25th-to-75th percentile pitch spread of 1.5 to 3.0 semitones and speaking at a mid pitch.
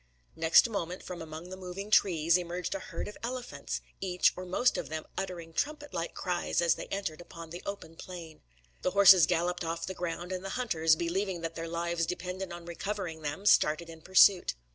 Yes: narrow, 2.5 semitones; medium, 175 Hz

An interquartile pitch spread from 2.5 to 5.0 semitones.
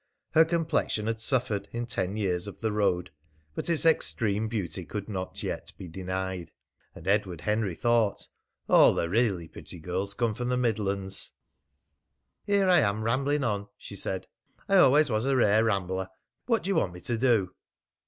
Yes: average, 4.5 semitones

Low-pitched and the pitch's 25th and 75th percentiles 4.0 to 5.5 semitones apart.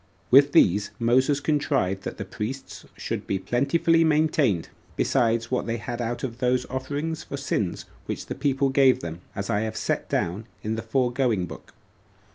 Yes: low, 125 Hz; average, 4.3 semitones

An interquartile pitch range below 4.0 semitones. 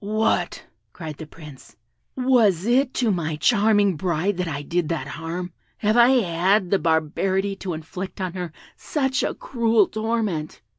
No: average, 5.1 semitones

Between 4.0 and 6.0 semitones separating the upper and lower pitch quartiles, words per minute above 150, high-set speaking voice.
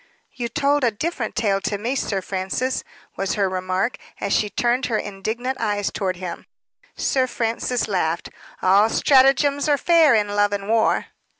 Yes: average, 4.5 semitones; average, 165 wpm; high, 220 Hz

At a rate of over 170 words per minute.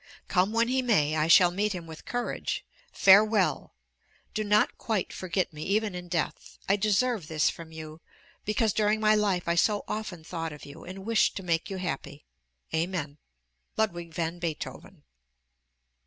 No: average, 165 wpm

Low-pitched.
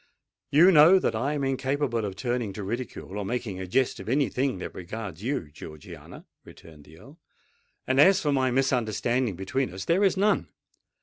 Yes: low, 125 Hz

